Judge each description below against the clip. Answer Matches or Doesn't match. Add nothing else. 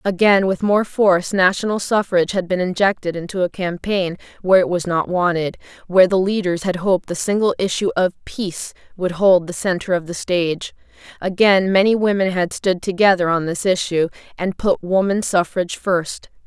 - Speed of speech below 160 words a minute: Doesn't match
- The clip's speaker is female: Matches